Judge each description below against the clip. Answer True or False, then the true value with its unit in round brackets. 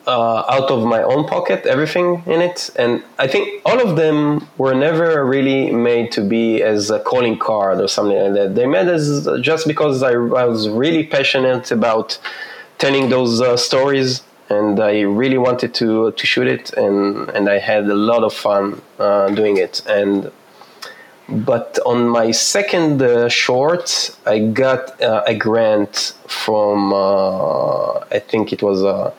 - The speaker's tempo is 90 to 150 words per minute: False (170 wpm)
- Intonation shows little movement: False (4.5 semitones)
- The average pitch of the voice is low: True (120 Hz)